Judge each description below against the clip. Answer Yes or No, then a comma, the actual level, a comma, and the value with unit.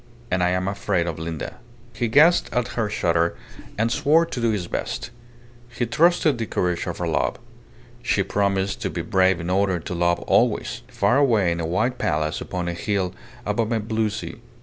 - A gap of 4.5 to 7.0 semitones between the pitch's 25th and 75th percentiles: Yes, average, 4.8 semitones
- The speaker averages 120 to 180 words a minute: No, average, 195 wpm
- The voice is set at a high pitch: No, low, 100 Hz